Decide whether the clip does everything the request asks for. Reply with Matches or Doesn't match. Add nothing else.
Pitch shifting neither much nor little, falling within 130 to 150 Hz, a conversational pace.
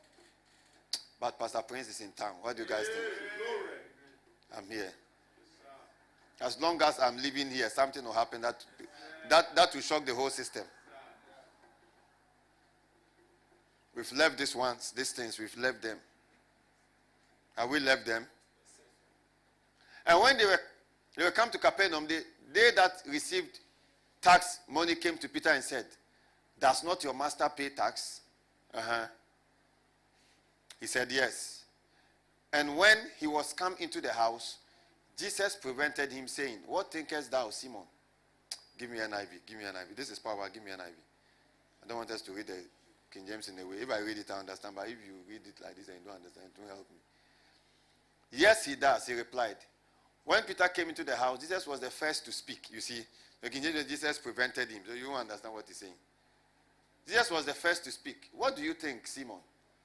Doesn't match